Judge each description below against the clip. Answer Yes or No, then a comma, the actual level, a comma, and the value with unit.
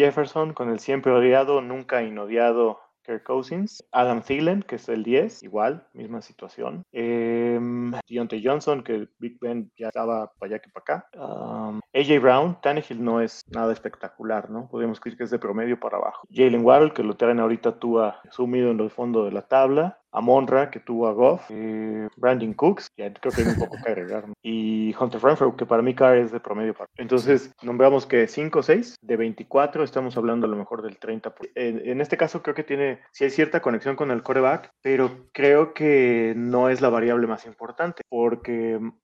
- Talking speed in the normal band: No, fast, 200 wpm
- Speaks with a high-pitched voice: No, low, 120 Hz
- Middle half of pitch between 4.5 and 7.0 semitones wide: No, average, 2.9 semitones